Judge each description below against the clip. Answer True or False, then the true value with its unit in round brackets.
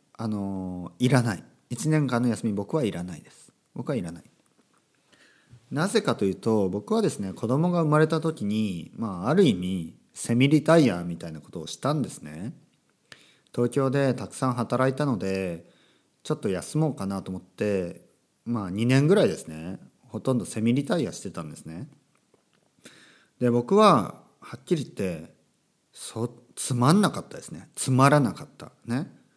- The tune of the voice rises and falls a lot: True (6.2 semitones)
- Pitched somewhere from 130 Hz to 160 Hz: False (120 Hz)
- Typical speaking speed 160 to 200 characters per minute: False (310 characters per minute)